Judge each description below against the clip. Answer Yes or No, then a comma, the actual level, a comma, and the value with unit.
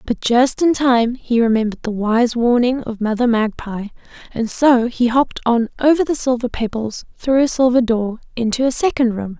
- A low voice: No, high, 240 Hz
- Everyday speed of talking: Yes, average, 185 wpm